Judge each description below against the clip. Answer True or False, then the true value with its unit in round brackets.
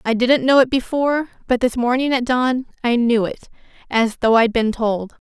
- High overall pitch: True (245 Hz)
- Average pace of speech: True (195 wpm)